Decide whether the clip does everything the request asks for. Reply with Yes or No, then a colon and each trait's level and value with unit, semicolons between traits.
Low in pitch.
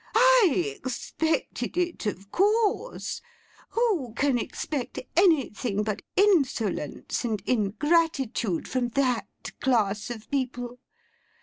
No: very high, 255 Hz